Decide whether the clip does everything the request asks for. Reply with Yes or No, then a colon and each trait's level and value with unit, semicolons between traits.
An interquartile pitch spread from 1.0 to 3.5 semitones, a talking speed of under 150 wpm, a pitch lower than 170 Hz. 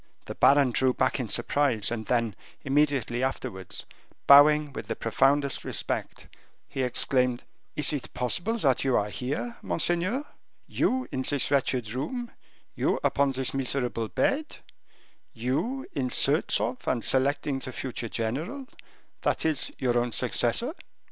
Yes: average, 3.2 semitones; average, 140 wpm; low, 135 Hz